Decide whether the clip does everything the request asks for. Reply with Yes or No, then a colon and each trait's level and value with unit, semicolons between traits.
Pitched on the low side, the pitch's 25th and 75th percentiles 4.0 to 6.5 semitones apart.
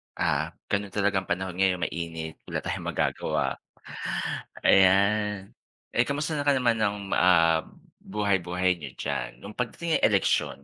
No: very low, 95 Hz; average, 3.2 semitones